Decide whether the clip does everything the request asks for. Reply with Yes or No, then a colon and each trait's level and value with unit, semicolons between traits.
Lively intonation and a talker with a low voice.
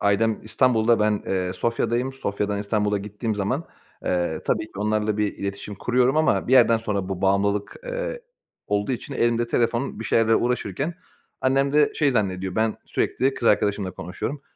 No: average, 3.6 semitones; low, 110 Hz